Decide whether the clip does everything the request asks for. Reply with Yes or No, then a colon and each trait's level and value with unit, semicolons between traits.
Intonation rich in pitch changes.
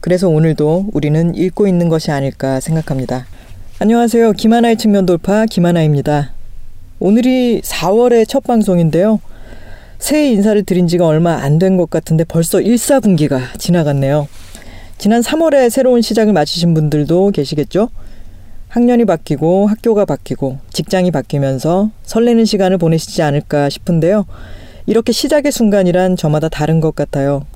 Yes: wide, 6.3 semitones